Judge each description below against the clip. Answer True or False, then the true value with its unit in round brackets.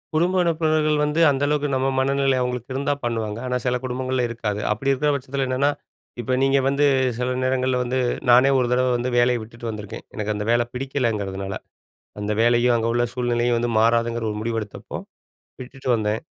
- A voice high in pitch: False (125 Hz)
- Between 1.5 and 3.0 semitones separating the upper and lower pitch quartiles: True (2.6 semitones)